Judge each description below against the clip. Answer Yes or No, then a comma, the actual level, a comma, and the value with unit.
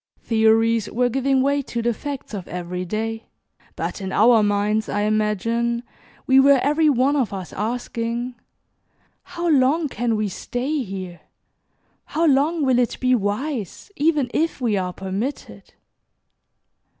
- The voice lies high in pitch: Yes, high, 235 Hz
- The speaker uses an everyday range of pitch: Yes, average, 4.5 semitones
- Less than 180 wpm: Yes, average, 140 wpm